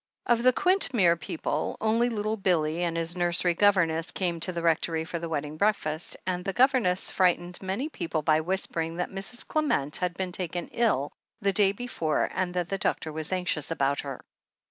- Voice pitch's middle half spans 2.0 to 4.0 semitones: Yes, average, 3.5 semitones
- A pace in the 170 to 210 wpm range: Yes, average, 185 wpm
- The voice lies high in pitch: No, medium, 180 Hz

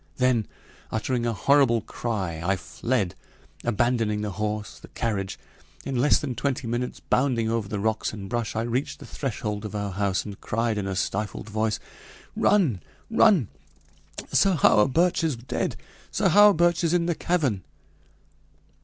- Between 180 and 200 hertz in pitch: No, low, 115 Hz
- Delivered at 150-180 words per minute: Yes, average, 155 wpm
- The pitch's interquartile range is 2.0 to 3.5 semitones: No, average, 4.6 semitones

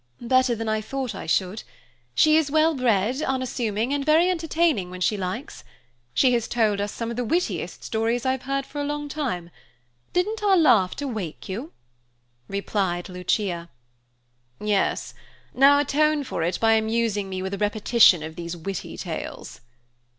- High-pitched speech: Yes, high, 230 Hz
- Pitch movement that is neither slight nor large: No, wide, 6.2 semitones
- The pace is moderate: Yes, average, 160 wpm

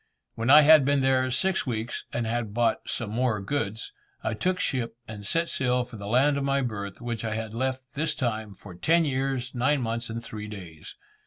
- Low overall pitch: Yes, low, 120 Hz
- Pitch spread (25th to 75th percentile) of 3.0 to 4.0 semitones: Yes, average, 3.5 semitones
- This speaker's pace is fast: Yes, fast, 210 wpm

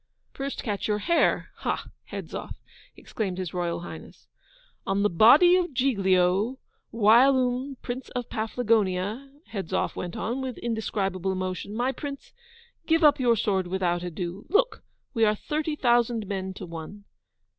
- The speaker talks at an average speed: Yes, average, 145 wpm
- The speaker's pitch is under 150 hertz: No, high, 220 Hz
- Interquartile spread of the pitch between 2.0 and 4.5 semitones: No, wide, 5.6 semitones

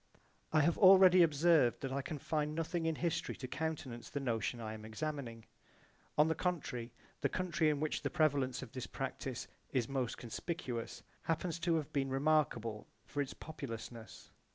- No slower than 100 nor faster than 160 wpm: No, average, 175 wpm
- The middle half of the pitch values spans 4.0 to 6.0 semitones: Yes, average, 4.8 semitones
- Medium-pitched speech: Yes, medium, 145 Hz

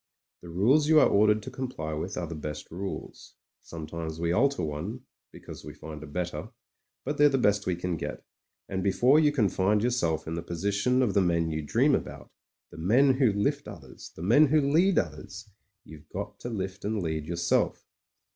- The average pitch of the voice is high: No, very low, 95 Hz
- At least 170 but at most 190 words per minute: No, fast, 205 wpm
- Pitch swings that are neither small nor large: No, wide, 7.0 semitones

